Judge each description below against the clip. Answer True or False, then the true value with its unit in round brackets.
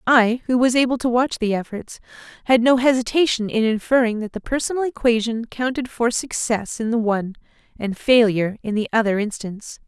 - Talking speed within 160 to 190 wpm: True (175 wpm)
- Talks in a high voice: True (235 Hz)